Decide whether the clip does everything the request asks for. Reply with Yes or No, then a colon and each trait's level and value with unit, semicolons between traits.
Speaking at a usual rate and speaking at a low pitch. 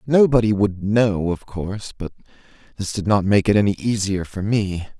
Yes: average, 180 wpm; low, 100 Hz